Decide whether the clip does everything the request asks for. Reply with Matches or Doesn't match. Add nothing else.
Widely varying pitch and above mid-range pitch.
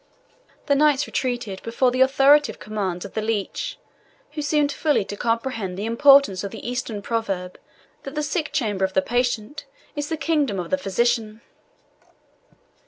Matches